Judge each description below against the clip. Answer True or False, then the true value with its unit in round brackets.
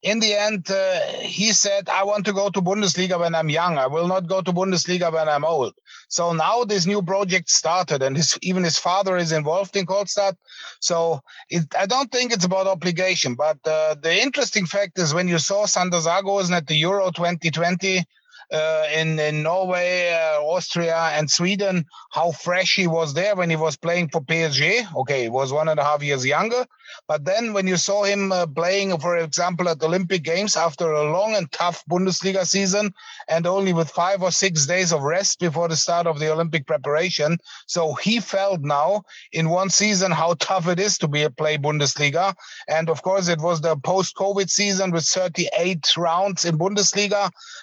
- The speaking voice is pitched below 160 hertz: False (175 Hz)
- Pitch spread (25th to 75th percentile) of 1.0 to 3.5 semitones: True (3.1 semitones)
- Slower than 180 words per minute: False (195 wpm)